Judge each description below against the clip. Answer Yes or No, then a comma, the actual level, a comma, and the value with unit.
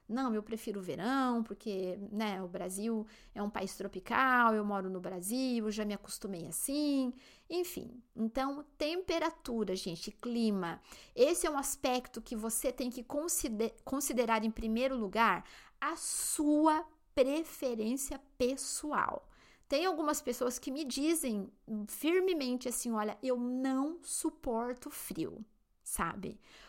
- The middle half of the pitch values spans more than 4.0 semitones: Yes, average, 4.8 semitones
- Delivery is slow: Yes, slow, 130 wpm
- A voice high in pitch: Yes, very high, 250 Hz